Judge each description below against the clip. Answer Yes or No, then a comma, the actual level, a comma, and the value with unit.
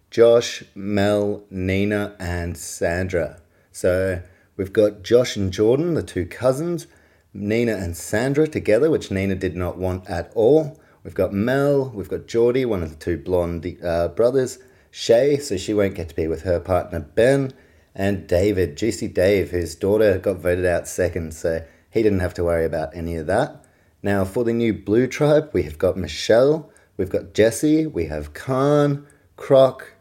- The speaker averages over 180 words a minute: No, average, 170 wpm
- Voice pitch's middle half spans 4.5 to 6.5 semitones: Yes, average, 5.3 semitones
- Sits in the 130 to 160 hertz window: No, low, 100 Hz